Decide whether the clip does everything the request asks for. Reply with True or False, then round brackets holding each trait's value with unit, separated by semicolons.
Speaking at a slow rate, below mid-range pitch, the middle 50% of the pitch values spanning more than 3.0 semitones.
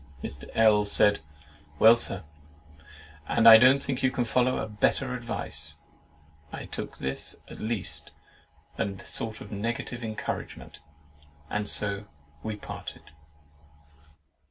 False (125 wpm; 110 Hz; 2.4 semitones)